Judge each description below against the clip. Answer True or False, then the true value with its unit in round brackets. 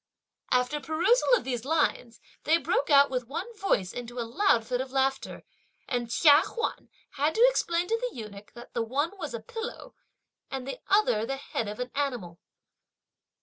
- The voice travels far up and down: True (5.9 semitones)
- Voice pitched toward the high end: True (270 Hz)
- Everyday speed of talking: True (180 wpm)